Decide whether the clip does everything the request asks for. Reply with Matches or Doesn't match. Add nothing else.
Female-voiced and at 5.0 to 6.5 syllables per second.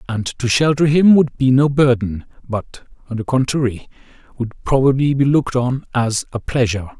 Doesn't match